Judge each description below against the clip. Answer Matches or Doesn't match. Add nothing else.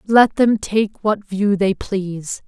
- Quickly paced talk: Doesn't match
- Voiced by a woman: Matches